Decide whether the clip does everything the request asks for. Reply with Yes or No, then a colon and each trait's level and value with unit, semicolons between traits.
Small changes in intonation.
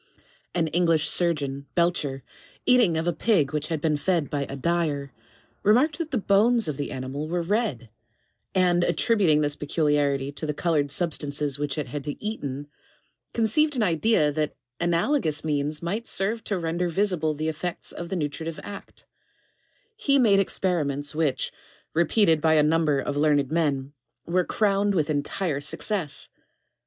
No: average, 4.6 semitones